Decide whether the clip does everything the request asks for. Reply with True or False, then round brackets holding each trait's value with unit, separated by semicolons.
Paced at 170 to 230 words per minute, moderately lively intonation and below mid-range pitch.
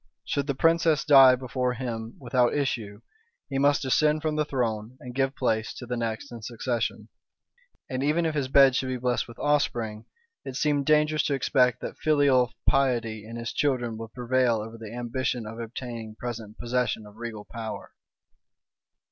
True (175 wpm; 3.2 semitones; 125 Hz)